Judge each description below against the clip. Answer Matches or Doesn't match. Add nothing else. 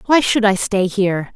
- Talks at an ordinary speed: Doesn't match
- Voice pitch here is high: Matches